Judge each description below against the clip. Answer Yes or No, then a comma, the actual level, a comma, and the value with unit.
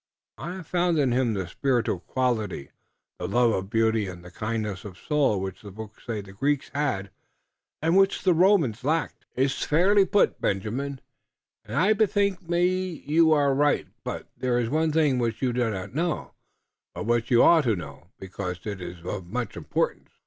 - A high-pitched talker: No, low, 125 Hz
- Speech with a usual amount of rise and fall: No, wide, 7.6 semitones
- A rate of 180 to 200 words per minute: Yes, average, 185 wpm